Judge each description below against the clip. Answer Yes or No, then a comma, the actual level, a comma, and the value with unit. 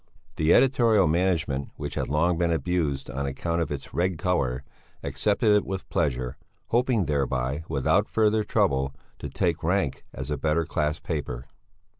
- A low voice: Yes, very low, 80 Hz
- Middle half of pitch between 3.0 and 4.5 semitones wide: No, average, 5.2 semitones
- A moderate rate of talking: Yes, average, 155 wpm